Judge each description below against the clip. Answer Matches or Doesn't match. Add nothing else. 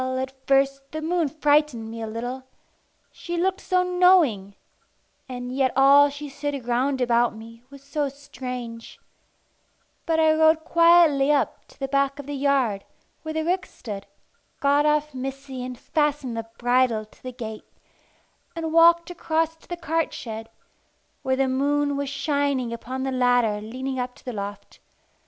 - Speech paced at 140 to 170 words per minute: Matches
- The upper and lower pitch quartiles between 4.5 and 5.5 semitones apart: Doesn't match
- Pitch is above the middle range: Matches